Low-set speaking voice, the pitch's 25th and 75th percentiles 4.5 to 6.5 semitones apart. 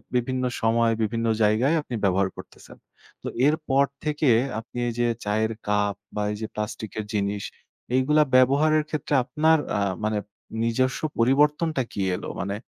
Yes: low, 120 Hz; wide, 5.5 semitones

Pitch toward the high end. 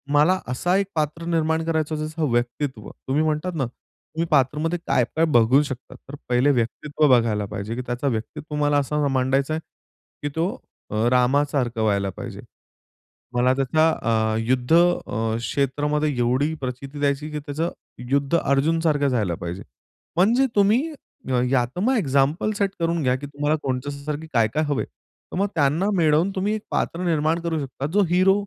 No: medium, 145 Hz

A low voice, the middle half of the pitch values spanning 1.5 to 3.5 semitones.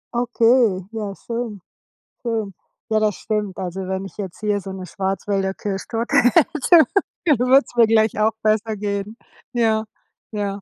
No: high, 215 Hz; average, 2.8 semitones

